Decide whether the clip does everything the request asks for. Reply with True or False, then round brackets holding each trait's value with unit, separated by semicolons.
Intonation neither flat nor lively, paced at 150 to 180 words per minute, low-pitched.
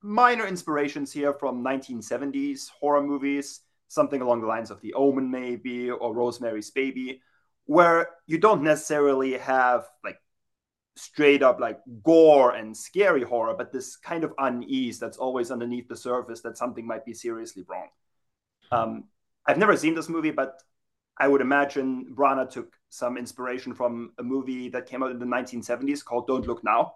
True (3.0 semitones; 165 wpm; 130 Hz)